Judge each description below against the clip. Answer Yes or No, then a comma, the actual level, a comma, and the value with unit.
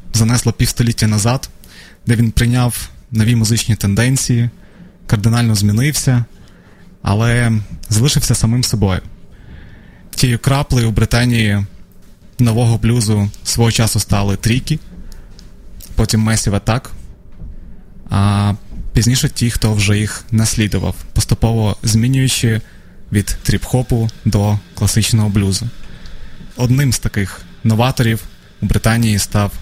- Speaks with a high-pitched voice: No, low, 110 Hz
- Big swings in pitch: No, average, 2.9 semitones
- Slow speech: Yes, slow, 100 wpm